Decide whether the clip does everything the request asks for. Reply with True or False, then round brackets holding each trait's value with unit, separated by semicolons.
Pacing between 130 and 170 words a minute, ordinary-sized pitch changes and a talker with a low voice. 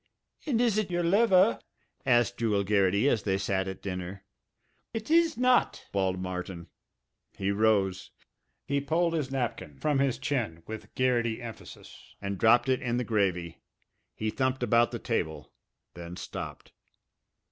False (145 wpm; 6.5 semitones; 115 Hz)